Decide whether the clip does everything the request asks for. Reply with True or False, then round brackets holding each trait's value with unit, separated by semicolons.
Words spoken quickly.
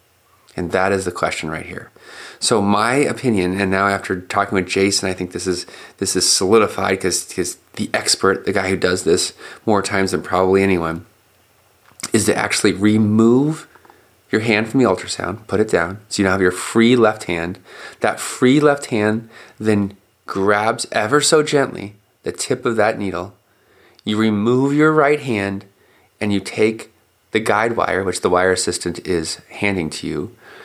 False (175 wpm)